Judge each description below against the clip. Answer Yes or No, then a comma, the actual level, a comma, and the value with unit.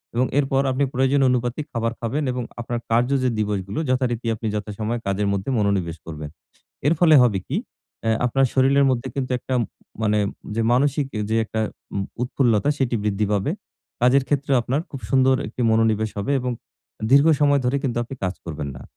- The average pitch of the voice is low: Yes, low, 120 Hz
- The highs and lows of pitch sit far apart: No, average, 4.0 semitones